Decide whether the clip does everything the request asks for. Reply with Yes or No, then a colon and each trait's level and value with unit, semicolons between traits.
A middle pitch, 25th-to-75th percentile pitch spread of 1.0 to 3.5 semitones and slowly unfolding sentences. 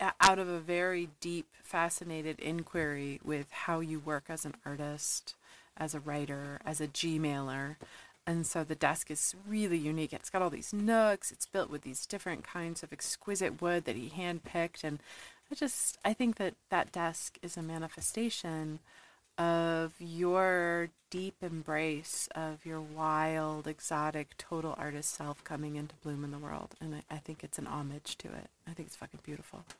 No: medium, 160 Hz; narrow, 2.6 semitones; average, 175 wpm